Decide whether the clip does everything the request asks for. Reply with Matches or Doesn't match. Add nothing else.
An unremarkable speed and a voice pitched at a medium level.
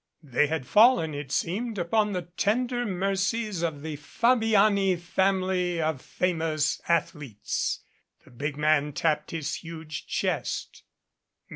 Doesn't match